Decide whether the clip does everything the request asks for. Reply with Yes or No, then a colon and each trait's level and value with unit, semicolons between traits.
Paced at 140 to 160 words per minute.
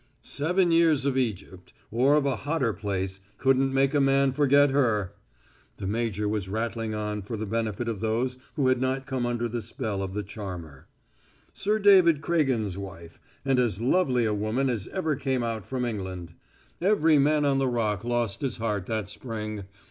No: average, 180 wpm